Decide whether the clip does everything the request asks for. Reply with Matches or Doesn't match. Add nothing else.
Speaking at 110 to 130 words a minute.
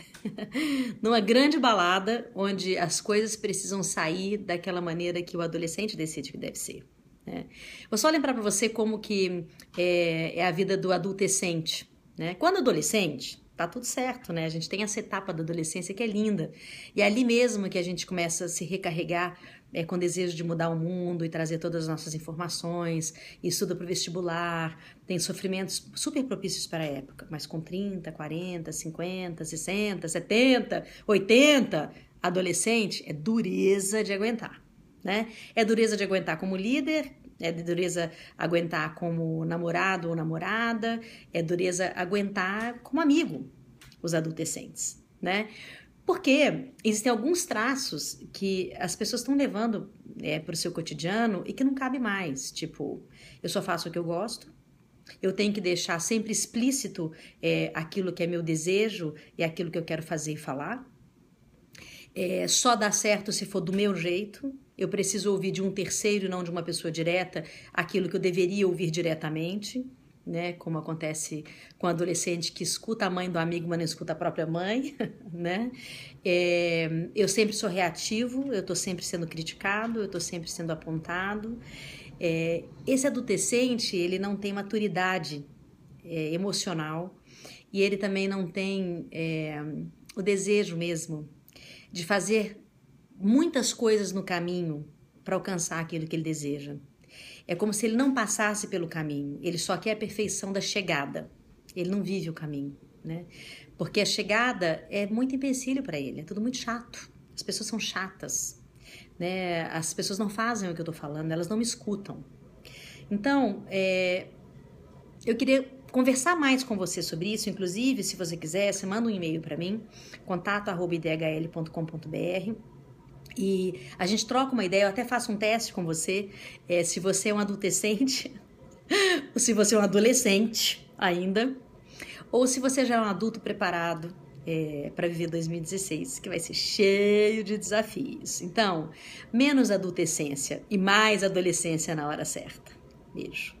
Doesn't match